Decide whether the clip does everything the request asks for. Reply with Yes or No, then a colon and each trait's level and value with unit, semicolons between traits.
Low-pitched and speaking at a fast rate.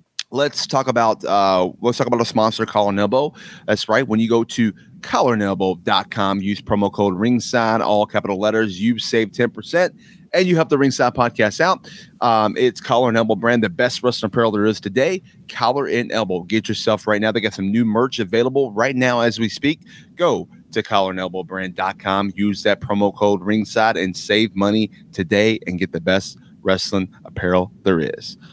No: low, 110 Hz; average, 185 wpm